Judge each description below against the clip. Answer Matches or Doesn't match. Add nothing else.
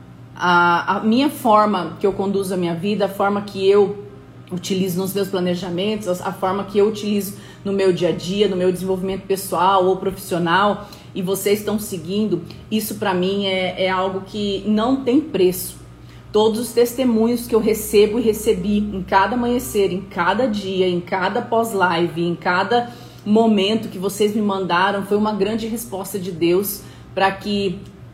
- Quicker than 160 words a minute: Matches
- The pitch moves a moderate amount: Doesn't match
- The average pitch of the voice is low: Doesn't match